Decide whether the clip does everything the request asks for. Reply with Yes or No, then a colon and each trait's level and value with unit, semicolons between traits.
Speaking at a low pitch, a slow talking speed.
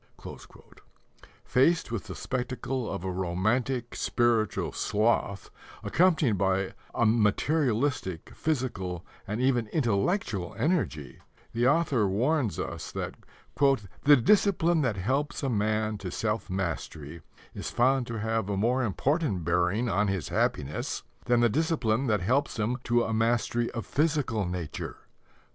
Yes: low, 115 Hz; slow, 130 wpm